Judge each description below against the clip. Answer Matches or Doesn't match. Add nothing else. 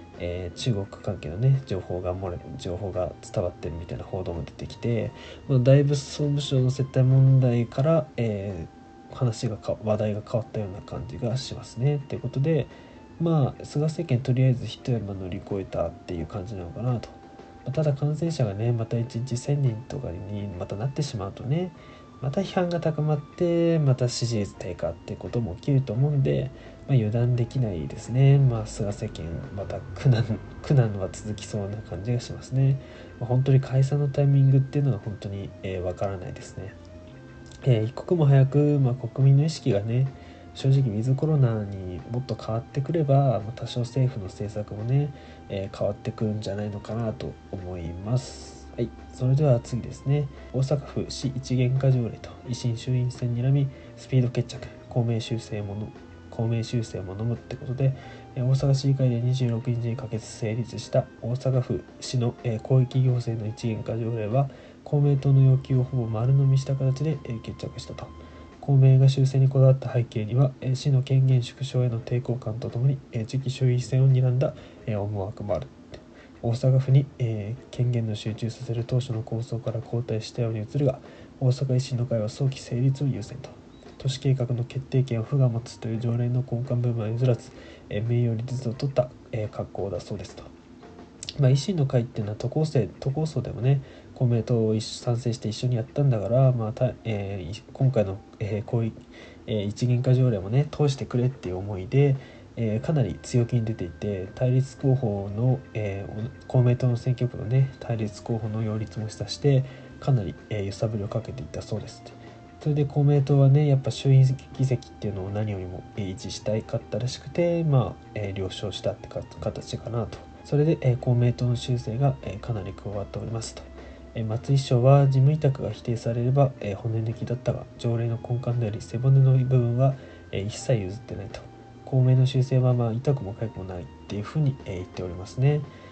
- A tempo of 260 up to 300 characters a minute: Doesn't match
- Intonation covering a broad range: Doesn't match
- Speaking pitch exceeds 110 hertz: Matches